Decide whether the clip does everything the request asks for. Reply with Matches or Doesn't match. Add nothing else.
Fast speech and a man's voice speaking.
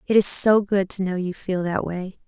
Doesn't match